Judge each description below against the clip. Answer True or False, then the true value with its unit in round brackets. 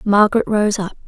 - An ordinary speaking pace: True (165 wpm)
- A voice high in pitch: True (205 Hz)